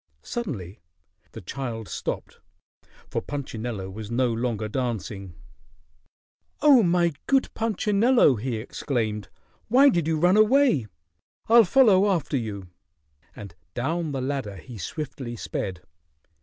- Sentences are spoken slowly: Yes, slow, 115 wpm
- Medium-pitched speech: No, low, 130 Hz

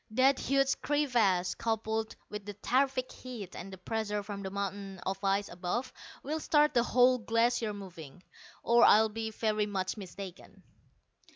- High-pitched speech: Yes, high, 215 Hz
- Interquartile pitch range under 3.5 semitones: No, average, 3.9 semitones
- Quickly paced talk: No, average, 155 wpm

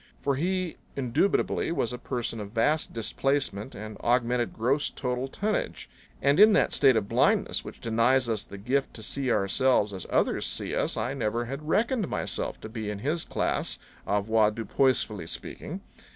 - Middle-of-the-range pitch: No, low, 125 Hz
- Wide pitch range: No, average, 4.3 semitones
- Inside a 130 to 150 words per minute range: No, average, 165 wpm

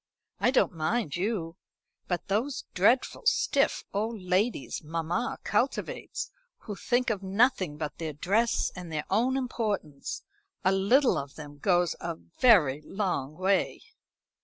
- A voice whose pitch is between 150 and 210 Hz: Yes, high, 190 Hz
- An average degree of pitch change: No, wide, 6.1 semitones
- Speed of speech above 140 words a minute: No, slow, 135 wpm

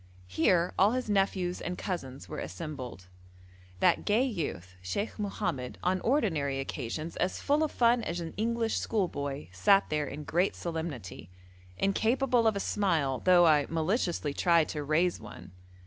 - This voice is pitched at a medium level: Yes, medium, 170 Hz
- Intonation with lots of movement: Yes, wide, 6.3 semitones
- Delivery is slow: No, average, 150 wpm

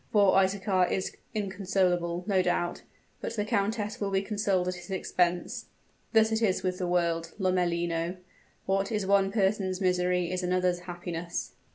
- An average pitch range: No, narrow, 1.9 semitones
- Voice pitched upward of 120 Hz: Yes, medium, 185 Hz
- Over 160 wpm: No, average, 155 wpm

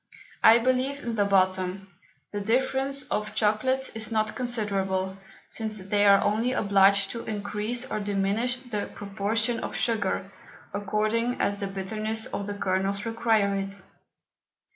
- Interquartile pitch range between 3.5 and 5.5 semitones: No, narrow, 2.6 semitones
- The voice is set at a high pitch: Yes, high, 210 Hz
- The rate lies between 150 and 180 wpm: No, average, 140 wpm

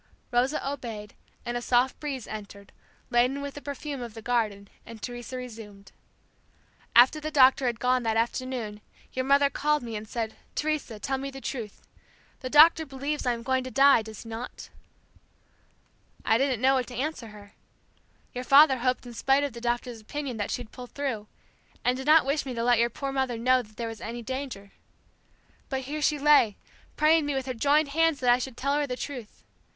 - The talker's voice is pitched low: No, very high, 255 Hz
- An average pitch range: Yes, average, 3.2 semitones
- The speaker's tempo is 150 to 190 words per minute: No, average, 200 wpm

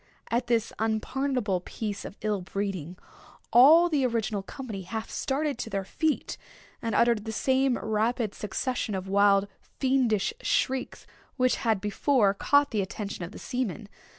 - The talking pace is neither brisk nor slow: Yes, average, 150 wpm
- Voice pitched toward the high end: Yes, high, 225 Hz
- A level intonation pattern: No, average, 4.3 semitones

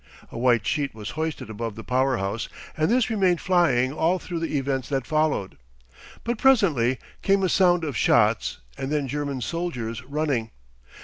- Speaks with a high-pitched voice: No, medium, 140 Hz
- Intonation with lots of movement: Yes, wide, 6.0 semitones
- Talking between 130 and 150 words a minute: No, average, 170 wpm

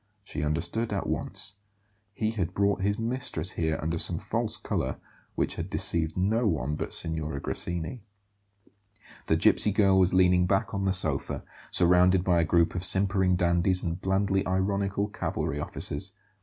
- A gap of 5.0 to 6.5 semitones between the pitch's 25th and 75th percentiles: No, average, 2.7 semitones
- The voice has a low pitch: Yes, very low, 95 Hz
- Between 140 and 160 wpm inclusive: Yes, average, 155 wpm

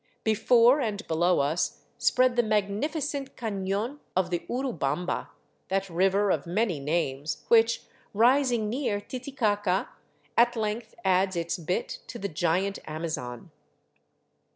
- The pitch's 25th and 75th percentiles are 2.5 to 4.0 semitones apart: No, average, 5.2 semitones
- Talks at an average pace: No, slow, 120 wpm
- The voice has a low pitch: No, high, 200 Hz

